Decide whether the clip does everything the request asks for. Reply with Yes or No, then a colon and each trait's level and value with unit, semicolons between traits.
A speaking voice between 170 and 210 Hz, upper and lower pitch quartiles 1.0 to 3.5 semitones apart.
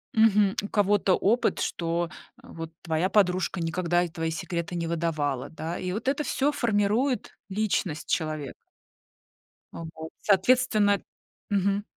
No: medium, 185 Hz; average, 4.0 semitones